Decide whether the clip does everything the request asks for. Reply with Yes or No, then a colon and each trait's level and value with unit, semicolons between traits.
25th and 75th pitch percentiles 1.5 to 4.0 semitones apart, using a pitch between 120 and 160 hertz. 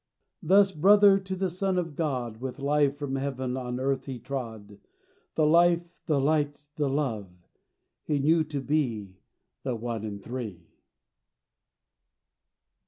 No: average, 4.5 semitones; medium, 140 Hz